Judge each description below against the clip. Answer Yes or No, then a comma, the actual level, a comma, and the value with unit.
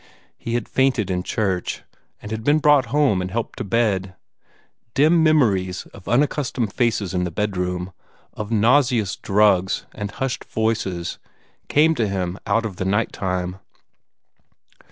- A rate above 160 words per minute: No, average, 145 wpm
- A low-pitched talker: Yes, low, 105 Hz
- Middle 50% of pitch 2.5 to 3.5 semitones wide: No, average, 4.6 semitones